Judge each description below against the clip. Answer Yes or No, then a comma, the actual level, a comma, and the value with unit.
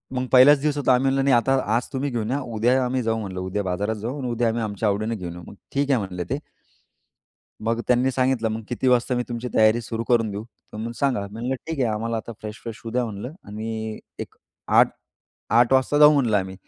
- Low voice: Yes, low, 115 Hz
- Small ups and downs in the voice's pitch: No, average, 3.1 semitones